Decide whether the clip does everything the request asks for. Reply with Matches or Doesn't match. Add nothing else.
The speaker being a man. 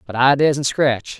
Matches